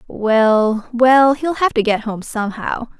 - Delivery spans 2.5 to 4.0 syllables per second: Yes, 3.7 syllables/s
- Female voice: Yes, female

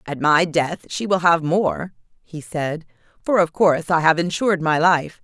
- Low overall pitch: No, medium, 165 Hz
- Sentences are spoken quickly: No, average, 195 wpm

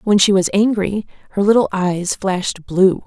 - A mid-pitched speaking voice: No, high, 195 Hz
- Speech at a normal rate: Yes, average, 175 wpm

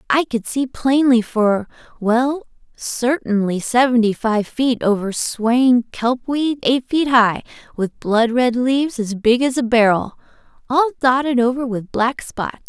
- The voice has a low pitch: No, high, 245 Hz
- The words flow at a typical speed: Yes, average, 150 wpm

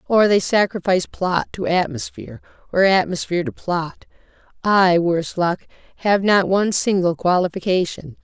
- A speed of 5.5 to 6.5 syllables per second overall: No, 5.0 syllables/s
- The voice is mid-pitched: Yes, medium, 180 Hz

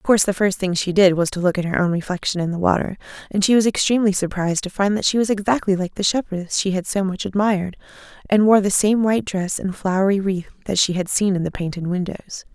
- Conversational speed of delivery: No, fast, 255 wpm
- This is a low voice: No, high, 195 Hz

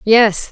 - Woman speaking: Yes, female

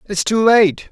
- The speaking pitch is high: Yes, high, 210 Hz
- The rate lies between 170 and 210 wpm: Yes, average, 200 wpm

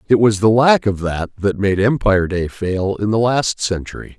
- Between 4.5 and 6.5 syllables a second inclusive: Yes, 4.7 syllables/s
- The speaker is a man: Yes, male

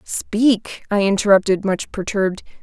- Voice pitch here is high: Yes, high, 200 Hz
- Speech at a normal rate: No, slow, 115 wpm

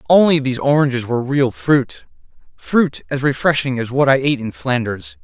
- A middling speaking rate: Yes, average, 170 wpm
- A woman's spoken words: No, male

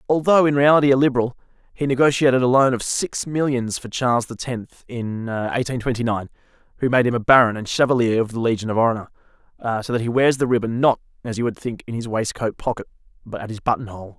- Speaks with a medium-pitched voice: No, low, 120 Hz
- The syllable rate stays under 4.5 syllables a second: No, 6.2 syllables/s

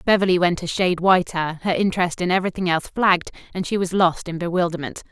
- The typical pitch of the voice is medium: Yes, medium, 175 Hz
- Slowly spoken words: No, average, 200 wpm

